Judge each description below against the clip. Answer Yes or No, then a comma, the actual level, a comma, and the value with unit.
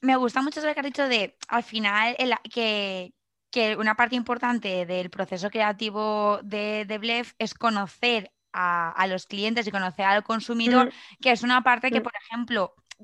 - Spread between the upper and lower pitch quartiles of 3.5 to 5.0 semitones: No, average, 2.9 semitones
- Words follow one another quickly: No, average, 180 wpm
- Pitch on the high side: Yes, high, 220 Hz